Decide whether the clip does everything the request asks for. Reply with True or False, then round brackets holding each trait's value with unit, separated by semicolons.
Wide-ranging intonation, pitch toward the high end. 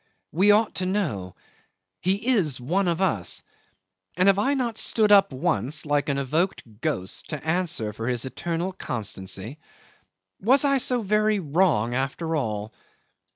False (8.0 semitones; 165 Hz)